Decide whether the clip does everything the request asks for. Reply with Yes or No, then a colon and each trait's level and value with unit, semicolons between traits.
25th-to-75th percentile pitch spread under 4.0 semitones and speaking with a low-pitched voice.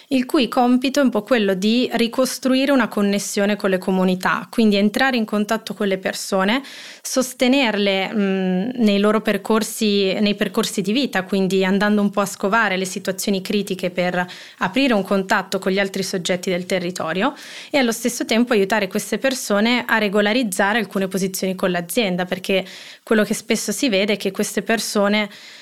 No: average, 3.0 semitones; high, 210 Hz